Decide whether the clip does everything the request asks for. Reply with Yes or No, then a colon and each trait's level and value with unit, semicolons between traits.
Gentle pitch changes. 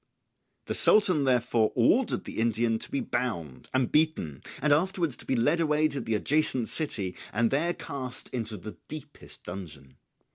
No: wide, 5.6 semitones